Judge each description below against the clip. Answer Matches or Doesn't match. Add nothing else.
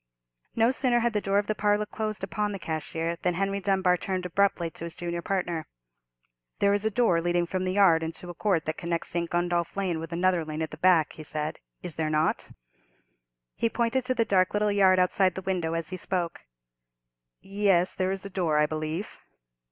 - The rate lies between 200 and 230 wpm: Matches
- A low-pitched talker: Doesn't match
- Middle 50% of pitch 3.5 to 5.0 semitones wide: Doesn't match